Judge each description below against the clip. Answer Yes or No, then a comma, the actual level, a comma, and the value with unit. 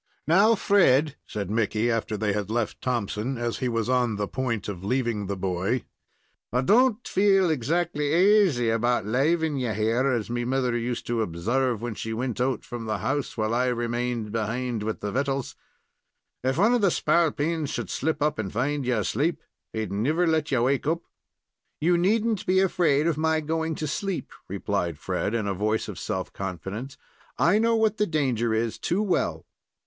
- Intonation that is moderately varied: No, wide, 6.3 semitones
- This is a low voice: Yes, low, 125 Hz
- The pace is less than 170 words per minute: No, average, 185 wpm